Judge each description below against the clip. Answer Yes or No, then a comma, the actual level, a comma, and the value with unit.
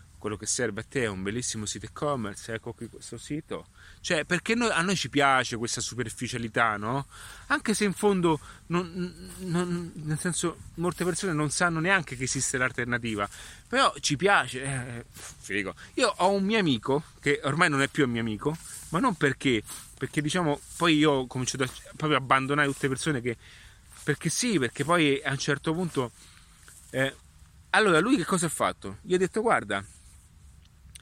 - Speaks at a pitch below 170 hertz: Yes, low, 135 Hz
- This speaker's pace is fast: Yes, fast, 185 wpm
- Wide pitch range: Yes, wide, 6.4 semitones